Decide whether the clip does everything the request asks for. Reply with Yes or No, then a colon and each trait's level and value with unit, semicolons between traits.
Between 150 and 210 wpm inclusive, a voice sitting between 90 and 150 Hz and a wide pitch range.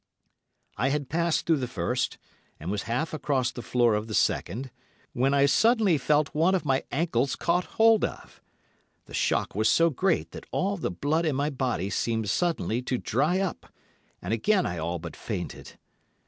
Yes: average, 180 wpm; medium, 140 Hz; wide, 6.4 semitones